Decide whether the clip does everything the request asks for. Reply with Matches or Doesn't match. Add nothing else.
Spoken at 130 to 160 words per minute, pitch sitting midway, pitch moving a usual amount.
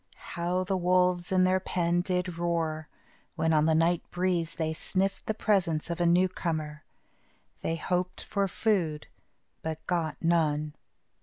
Doesn't match